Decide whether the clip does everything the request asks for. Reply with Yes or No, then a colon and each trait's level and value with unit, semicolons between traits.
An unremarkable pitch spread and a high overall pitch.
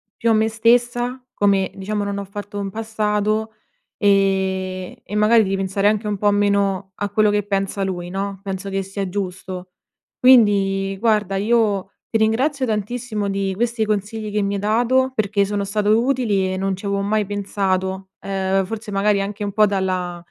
No: narrow, 1.9 semitones; high, 205 Hz